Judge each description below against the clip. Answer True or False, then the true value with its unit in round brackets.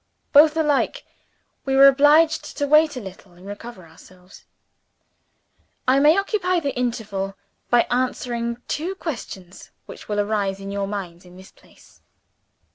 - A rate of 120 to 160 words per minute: True (140 wpm)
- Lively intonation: True (7.0 semitones)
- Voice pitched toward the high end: True (240 Hz)